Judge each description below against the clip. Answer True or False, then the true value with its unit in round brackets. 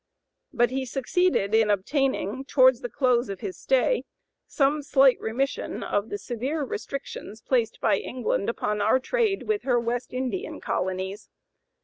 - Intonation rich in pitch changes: False (3.9 semitones)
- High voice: True (255 Hz)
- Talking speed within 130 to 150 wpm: True (145 wpm)